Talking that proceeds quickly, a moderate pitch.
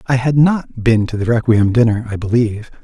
No: fast, 210 wpm; low, 115 Hz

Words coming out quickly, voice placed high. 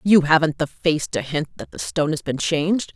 No: fast, 245 wpm; medium, 160 Hz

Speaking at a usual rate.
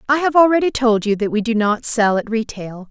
No: fast, 250 wpm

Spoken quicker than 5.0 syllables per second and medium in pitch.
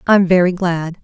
No: 4.7 syllables/s; medium, 180 Hz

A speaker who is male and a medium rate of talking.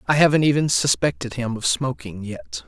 Yes: male; average, 180 wpm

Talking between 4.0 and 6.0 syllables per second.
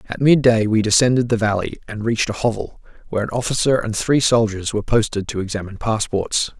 No: 6.2 syllables/s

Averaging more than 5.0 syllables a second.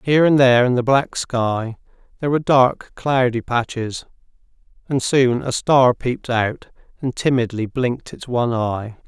No: 4.8 syllables/s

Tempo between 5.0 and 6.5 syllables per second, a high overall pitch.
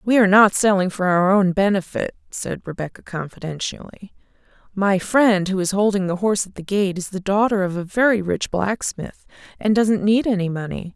Yes: 5.2 syllables/s; high, 195 Hz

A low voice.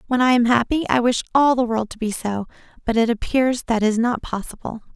No: high, 235 Hz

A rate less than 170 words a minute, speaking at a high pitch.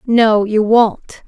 Yes: average, 140 wpm; high, 220 Hz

